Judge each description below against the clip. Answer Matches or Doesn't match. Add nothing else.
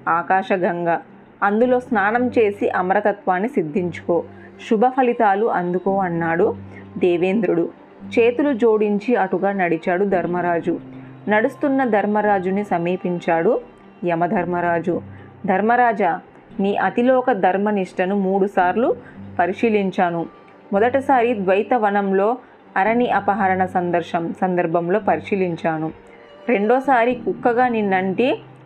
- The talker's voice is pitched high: Matches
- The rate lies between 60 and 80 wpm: Matches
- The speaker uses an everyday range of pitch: Matches